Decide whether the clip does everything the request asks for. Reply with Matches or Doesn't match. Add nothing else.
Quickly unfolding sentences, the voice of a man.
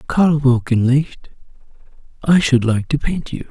Doesn't match